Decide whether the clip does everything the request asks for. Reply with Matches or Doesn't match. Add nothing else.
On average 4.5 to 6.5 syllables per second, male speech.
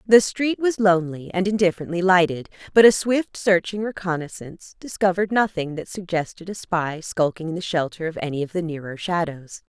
Doesn't match